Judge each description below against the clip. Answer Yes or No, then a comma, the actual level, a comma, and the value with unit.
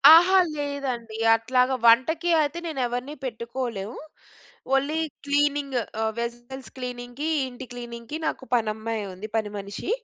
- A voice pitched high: Yes, very high, 250 Hz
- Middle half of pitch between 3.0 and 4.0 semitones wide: Yes, average, 3.6 semitones